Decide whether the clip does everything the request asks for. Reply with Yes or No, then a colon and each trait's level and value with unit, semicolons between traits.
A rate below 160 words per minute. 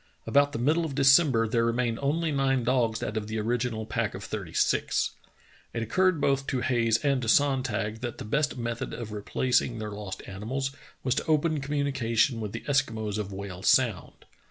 No: average, 185 wpm